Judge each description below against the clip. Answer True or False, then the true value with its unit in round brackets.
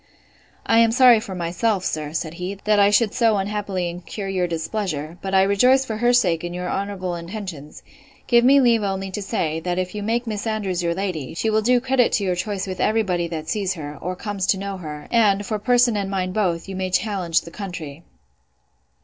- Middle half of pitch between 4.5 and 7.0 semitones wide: False (3.6 semitones)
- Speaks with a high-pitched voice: True (195 Hz)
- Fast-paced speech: True (215 wpm)